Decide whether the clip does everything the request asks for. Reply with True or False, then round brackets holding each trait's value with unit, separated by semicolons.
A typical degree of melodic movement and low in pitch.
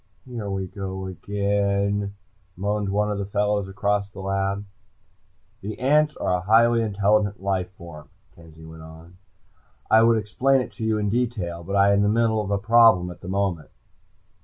False (2.0 semitones; 100 Hz)